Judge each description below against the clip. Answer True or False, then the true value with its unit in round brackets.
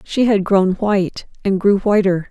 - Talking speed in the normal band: True (185 wpm)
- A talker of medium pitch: False (195 Hz)